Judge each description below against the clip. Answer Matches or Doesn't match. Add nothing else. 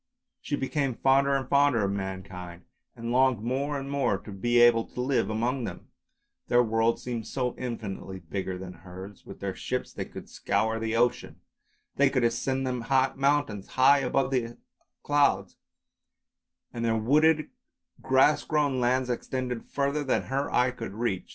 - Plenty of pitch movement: Doesn't match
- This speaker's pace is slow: Doesn't match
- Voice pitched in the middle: Doesn't match